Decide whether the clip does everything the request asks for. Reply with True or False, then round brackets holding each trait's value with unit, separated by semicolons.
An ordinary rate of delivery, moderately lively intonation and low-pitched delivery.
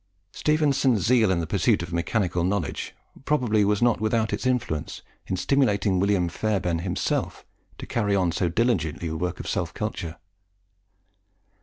True (150 wpm; 5.0 semitones; 100 Hz)